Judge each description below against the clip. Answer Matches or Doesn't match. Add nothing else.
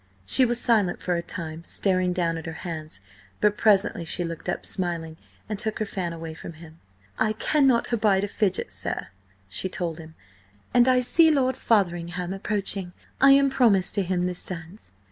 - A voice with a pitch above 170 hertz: Matches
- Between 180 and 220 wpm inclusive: Matches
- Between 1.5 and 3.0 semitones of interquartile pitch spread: Doesn't match